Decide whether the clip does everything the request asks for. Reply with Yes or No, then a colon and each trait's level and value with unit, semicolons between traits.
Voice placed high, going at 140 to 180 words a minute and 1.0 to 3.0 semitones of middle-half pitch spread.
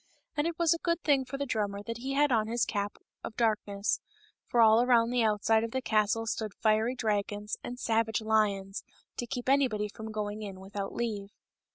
No: high, 220 Hz; average, 195 wpm; average, 2.7 semitones